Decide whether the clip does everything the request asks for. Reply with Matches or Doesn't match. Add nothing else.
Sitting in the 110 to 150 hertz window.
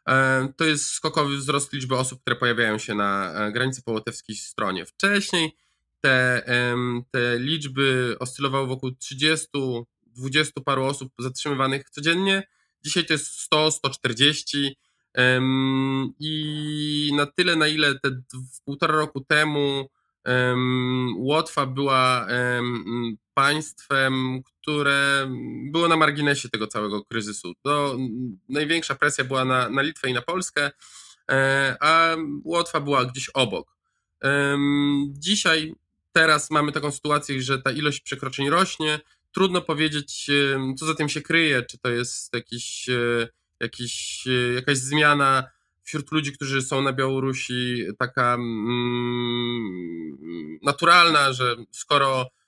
Matches